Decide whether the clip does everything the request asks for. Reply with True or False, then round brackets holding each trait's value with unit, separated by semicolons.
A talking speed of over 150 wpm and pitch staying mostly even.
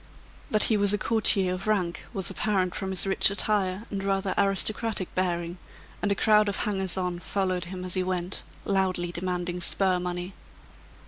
True (175 wpm; 1.9 semitones)